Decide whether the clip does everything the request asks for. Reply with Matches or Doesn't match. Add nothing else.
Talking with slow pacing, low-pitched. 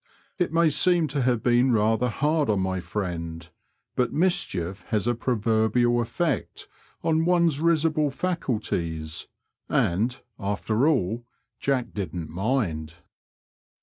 Matches